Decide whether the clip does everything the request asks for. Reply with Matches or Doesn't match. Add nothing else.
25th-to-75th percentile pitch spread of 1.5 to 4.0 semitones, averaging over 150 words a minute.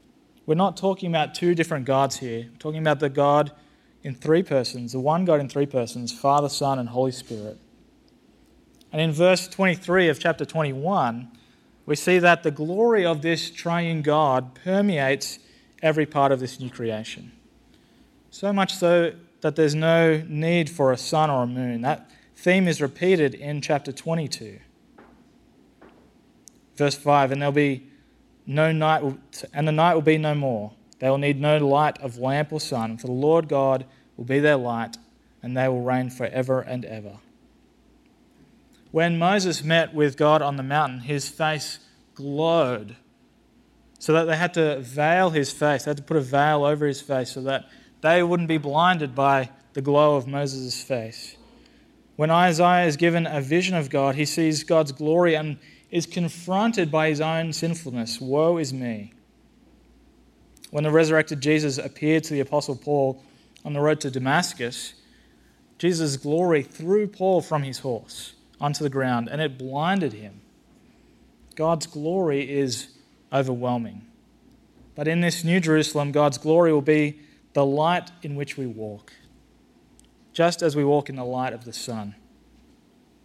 Matches